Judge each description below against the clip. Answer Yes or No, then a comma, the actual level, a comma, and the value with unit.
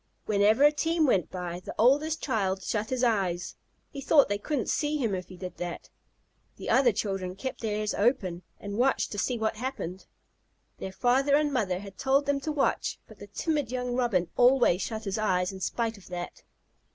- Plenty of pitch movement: Yes, wide, 5.9 semitones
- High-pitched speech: Yes, high, 220 Hz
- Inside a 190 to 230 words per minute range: Yes, average, 195 wpm